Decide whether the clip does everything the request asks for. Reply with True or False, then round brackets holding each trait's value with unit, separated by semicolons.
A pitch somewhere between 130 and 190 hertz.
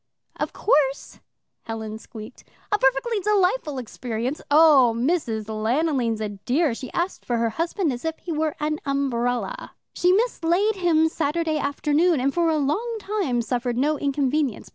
False (290 Hz)